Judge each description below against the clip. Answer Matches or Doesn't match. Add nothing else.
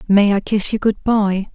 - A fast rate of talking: Matches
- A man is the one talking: Doesn't match